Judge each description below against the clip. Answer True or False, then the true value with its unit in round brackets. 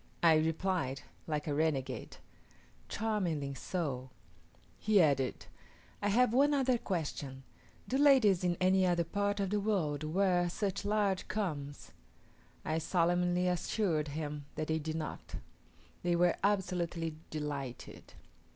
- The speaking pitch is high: False (175 Hz)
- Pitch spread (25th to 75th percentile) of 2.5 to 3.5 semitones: False (4.7 semitones)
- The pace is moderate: False (125 wpm)